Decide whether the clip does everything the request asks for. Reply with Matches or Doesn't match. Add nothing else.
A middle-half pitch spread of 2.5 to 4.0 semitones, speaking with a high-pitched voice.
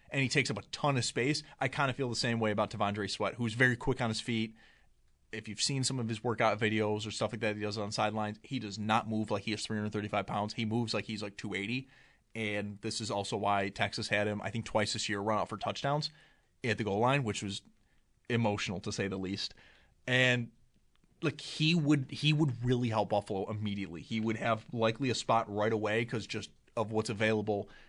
Doesn't match